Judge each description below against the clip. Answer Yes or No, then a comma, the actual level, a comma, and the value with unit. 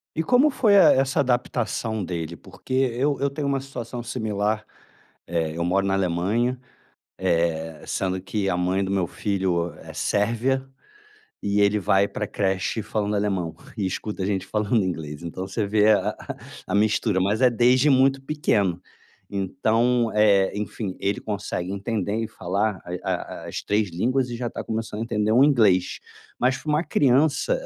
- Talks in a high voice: No, low, 105 Hz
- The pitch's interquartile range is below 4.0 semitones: No, average, 4.5 semitones